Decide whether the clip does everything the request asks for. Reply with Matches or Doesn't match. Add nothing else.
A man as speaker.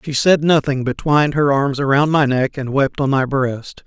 Matches